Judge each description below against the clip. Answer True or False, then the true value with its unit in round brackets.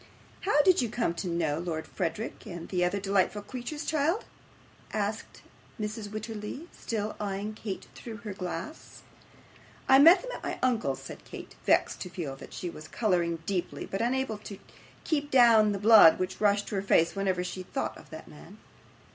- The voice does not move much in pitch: False (4.4 semitones)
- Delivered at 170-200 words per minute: True (180 wpm)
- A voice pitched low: False (205 Hz)